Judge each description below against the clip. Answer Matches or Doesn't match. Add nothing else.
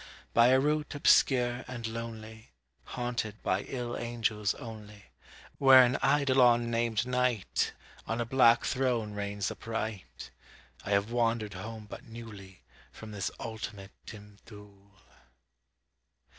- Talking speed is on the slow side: Matches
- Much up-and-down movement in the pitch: Doesn't match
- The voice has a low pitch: Matches